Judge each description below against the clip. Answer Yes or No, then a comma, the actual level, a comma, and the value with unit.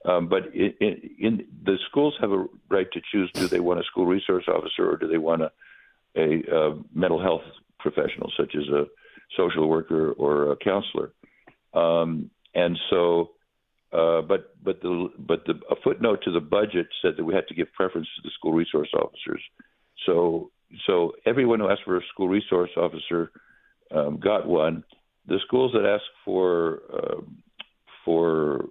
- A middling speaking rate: Yes, average, 175 wpm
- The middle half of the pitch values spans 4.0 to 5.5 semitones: Yes, average, 4.5 semitones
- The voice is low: Yes, very low, 85 Hz